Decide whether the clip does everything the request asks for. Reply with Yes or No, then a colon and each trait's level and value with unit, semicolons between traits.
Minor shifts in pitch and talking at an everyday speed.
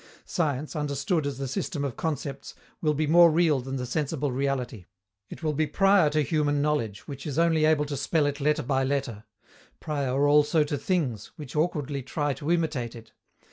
Yes: narrow, 2.3 semitones; average, 185 wpm